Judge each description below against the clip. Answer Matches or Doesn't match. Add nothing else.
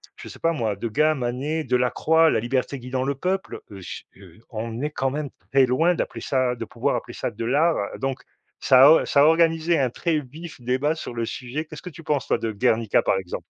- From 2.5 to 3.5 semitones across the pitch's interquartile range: Doesn't match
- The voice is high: Doesn't match